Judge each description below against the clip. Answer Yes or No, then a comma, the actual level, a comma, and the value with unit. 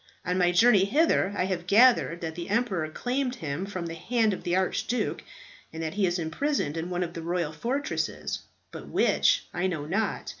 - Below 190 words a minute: No, average, 195 wpm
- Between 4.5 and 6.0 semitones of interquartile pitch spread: Yes, average, 5.2 semitones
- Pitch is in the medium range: Yes, medium, 180 Hz